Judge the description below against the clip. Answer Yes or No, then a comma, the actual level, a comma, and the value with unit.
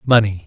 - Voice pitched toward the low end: Yes, low, 105 Hz